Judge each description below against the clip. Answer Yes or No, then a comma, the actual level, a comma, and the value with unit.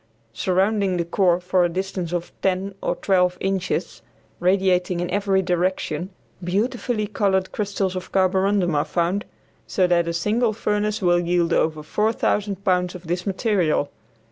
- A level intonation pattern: Yes, narrow, 2.2 semitones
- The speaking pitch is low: No, medium, 185 Hz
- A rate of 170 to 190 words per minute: No, average, 145 wpm